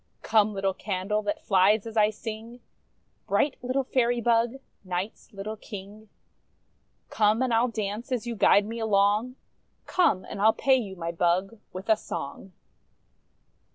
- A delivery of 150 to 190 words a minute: Yes, average, 155 wpm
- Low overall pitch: No, high, 215 Hz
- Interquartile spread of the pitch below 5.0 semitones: Yes, average, 2.8 semitones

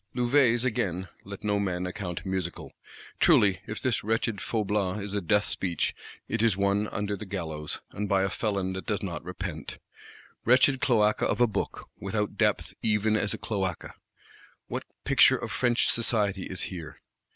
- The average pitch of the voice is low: Yes, low, 100 Hz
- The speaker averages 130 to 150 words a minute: No, average, 165 wpm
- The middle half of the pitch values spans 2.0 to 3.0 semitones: Yes, narrow, 2.5 semitones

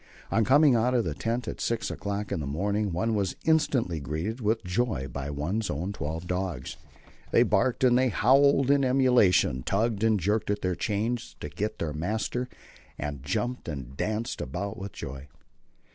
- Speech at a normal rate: Yes, average, 175 wpm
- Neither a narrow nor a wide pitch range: No, wide, 6.5 semitones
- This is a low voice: Yes, low, 105 Hz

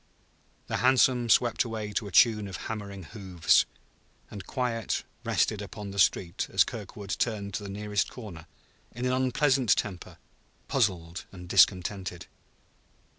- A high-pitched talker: No, low, 105 Hz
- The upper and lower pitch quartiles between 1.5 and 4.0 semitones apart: Yes, average, 3.6 semitones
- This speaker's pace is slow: Yes, slow, 130 wpm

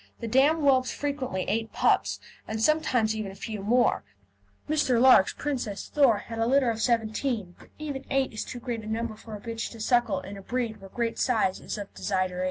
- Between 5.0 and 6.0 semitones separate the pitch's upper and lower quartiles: No, average, 3.2 semitones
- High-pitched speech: Yes, high, 230 Hz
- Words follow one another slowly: No, fast, 205 wpm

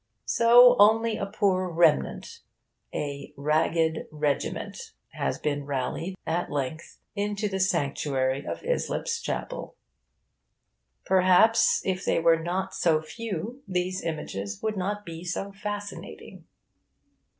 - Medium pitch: Yes, medium, 180 Hz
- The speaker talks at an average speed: No, slow, 115 wpm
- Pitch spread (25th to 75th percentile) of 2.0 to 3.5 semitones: No, average, 5.1 semitones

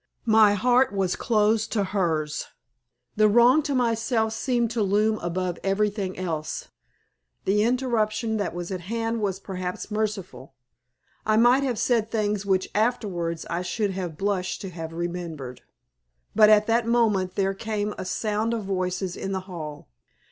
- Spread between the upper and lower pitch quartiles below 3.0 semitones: No, average, 3.4 semitones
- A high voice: Yes, high, 205 Hz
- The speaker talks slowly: No, average, 155 wpm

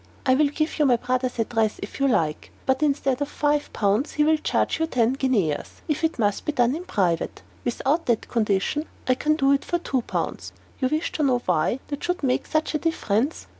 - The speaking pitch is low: No, very high, 265 Hz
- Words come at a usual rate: No, fast, 215 wpm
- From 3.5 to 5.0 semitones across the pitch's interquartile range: Yes, average, 4.6 semitones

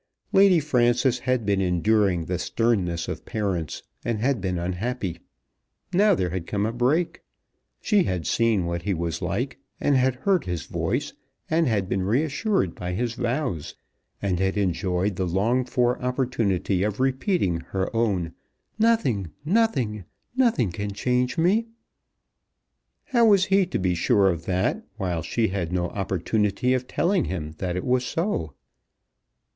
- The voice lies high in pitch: No, low, 105 Hz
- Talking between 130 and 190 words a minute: Yes, average, 150 wpm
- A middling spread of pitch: No, wide, 6.0 semitones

